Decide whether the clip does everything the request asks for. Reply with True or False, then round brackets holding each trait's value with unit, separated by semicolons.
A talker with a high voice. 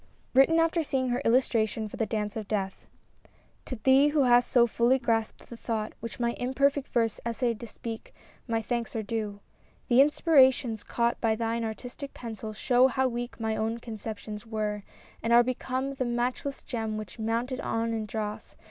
True (235 Hz)